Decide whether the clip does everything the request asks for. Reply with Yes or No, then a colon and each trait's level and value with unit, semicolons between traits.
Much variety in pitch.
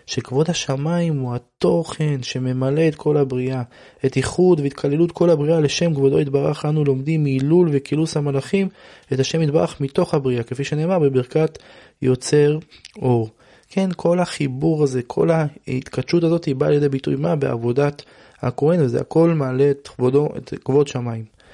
No: average, 3.6 semitones